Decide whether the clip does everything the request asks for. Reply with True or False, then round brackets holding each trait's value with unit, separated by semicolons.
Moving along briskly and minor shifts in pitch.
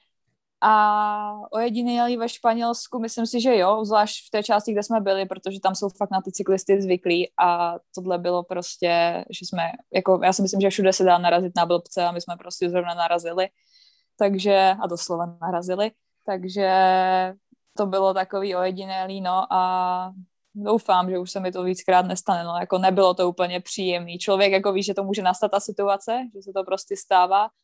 True (185 wpm; 2.3 semitones)